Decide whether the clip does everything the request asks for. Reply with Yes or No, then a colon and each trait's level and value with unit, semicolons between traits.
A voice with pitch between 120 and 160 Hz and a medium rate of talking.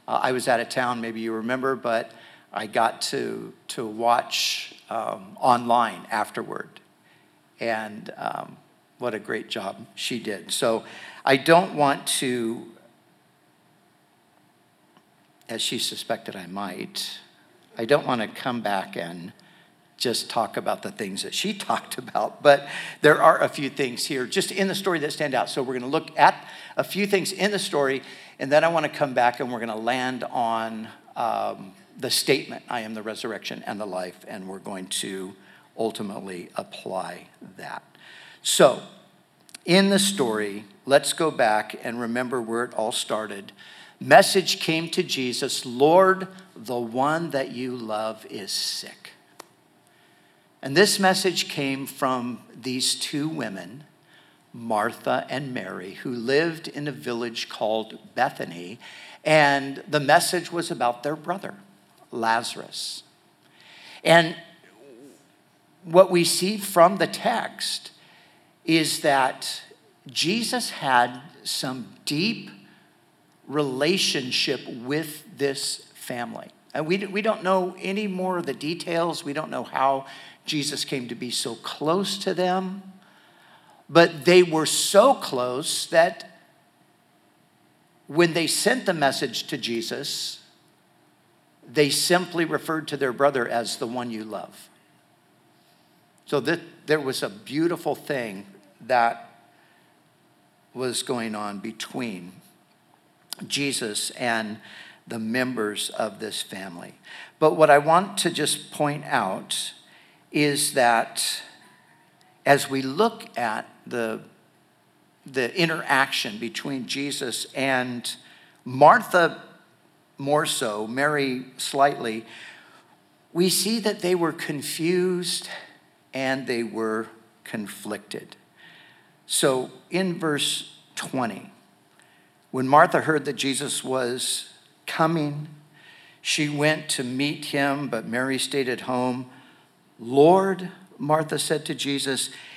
No: medium, 140 Hz; slow, 125 wpm